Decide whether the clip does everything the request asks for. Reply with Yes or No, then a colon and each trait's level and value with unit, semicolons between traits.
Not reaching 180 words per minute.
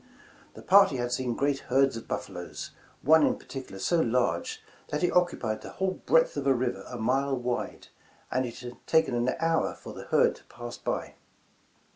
No: average, 185 wpm